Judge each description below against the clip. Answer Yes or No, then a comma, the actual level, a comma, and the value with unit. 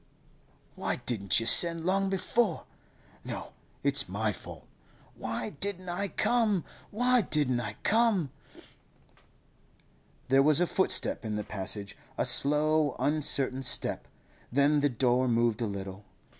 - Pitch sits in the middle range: Yes, medium, 145 Hz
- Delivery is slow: Yes, slow, 130 wpm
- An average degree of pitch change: No, wide, 7.7 semitones